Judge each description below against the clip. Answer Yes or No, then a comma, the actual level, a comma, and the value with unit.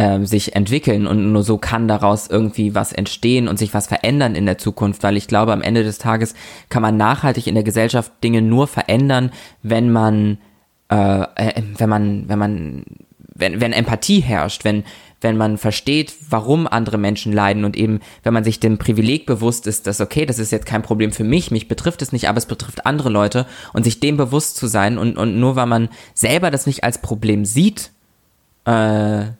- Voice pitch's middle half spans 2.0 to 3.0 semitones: Yes, narrow, 2.4 semitones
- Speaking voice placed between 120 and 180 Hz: No, low, 110 Hz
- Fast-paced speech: Yes, fast, 200 wpm